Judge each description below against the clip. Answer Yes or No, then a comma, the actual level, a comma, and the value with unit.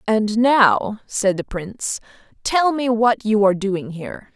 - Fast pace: No, average, 165 wpm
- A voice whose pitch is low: No, high, 215 Hz